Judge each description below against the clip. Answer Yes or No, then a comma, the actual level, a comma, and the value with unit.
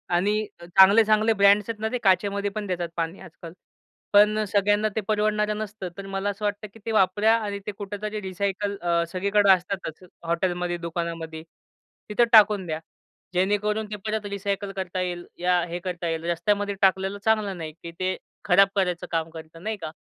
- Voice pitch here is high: Yes, high, 195 Hz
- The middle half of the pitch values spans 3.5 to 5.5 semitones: No, average, 2.9 semitones